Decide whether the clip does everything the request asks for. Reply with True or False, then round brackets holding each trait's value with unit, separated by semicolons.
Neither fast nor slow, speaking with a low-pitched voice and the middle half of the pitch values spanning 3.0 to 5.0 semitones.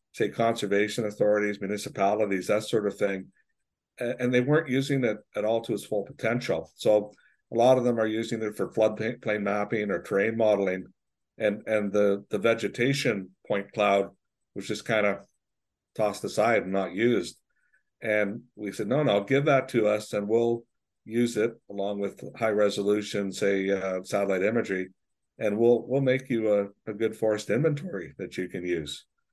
False (175 wpm; 105 Hz; 2.6 semitones)